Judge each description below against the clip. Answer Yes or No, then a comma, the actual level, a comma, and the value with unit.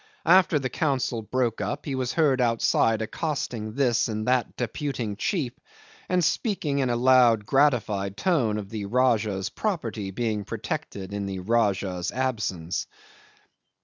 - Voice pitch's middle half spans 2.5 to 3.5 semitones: No, average, 4.4 semitones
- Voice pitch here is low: Yes, low, 120 Hz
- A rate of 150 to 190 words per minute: No, average, 140 wpm